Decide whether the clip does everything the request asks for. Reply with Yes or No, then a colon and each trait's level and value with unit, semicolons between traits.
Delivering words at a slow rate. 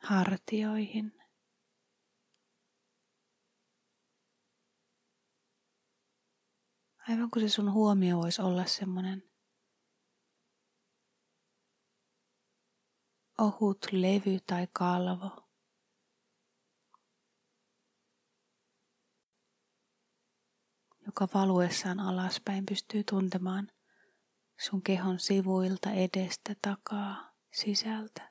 Yes: slow, 50 wpm